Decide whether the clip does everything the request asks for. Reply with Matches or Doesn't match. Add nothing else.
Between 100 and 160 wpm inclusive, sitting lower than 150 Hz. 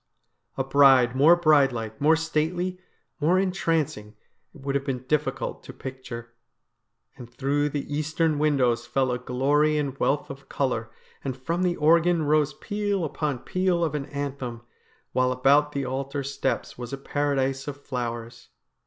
Matches